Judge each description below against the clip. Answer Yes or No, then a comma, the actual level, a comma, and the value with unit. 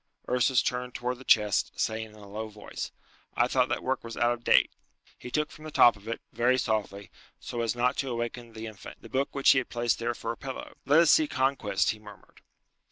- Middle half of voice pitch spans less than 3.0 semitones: Yes, narrow, 2.6 semitones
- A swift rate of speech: Yes, fast, 230 wpm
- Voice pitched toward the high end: No, low, 120 Hz